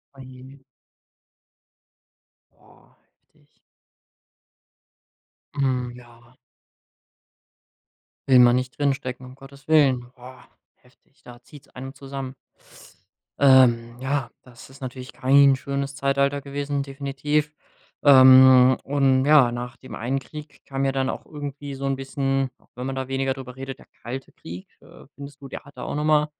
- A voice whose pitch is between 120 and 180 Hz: Yes, low, 135 Hz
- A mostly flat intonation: Yes, narrow, 1.5 semitones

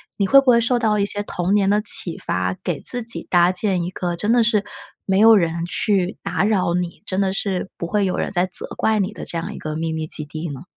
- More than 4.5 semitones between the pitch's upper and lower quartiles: No, average, 3.4 semitones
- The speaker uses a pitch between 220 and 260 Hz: No, high, 190 Hz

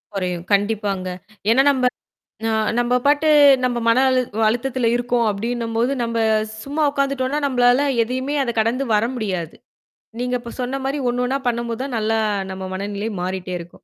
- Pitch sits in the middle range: No, high, 240 Hz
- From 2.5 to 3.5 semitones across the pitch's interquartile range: Yes, average, 3.2 semitones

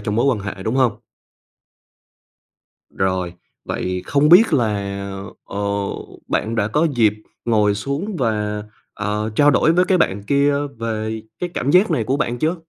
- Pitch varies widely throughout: Yes, wide, 5.7 semitones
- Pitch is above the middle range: No, low, 115 Hz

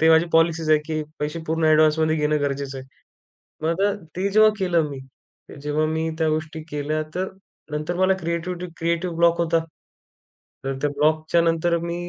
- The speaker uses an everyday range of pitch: No, narrow, 1.8 semitones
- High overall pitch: No, medium, 160 Hz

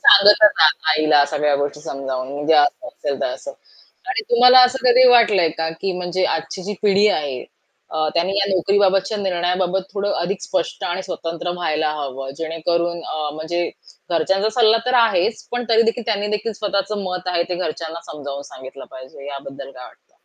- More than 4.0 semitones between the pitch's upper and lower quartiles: Yes, average, 4.9 semitones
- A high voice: No, medium, 175 Hz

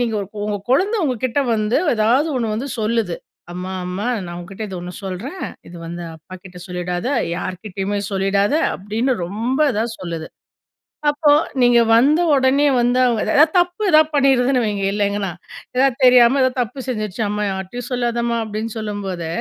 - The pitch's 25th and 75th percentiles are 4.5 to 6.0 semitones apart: Yes, average, 5.0 semitones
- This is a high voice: Yes, high, 220 Hz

